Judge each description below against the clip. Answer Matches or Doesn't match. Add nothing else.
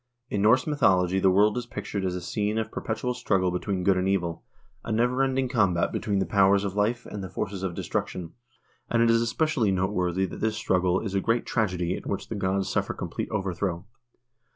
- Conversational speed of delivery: Doesn't match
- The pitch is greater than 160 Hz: Doesn't match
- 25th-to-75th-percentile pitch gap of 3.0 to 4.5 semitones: Matches